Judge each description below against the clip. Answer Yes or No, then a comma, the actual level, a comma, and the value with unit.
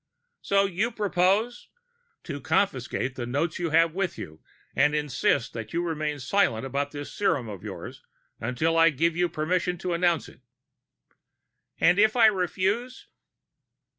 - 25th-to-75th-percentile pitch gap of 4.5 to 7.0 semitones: Yes, wide, 5.4 semitones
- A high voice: No, medium, 165 Hz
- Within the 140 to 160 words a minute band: Yes, average, 155 wpm